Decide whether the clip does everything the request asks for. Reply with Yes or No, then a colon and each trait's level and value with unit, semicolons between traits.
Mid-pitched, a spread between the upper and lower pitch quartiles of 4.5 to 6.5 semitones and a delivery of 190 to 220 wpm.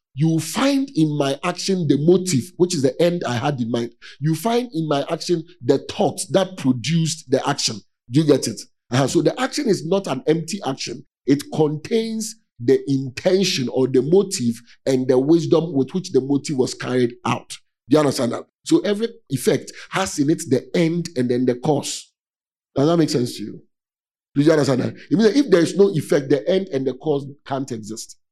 Yes: medium, 150 Hz; wide, 5.4 semitones; average, 200 wpm